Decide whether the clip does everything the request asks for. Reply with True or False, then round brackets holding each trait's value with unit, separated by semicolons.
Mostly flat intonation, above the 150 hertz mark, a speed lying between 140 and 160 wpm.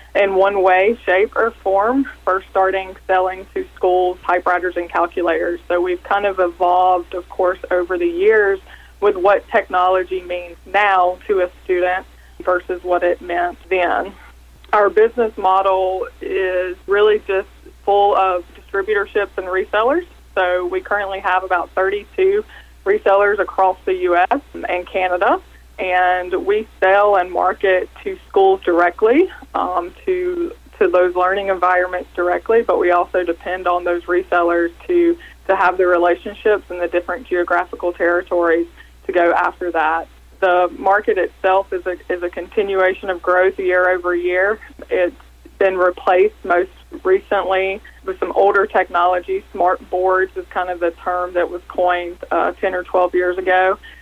True (2.1 semitones; 185 Hz; 150 wpm)